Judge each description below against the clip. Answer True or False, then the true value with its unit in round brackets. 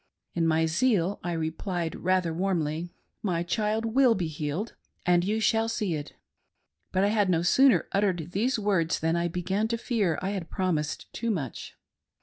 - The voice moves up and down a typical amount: True (4.2 semitones)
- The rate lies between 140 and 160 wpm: False (175 wpm)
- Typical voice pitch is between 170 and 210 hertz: True (185 Hz)